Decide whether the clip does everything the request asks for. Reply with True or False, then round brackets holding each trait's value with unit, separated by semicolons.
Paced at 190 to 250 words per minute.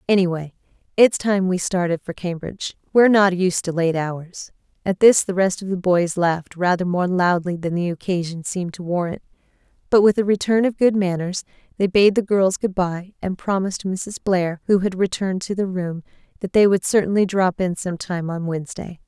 True (200 wpm)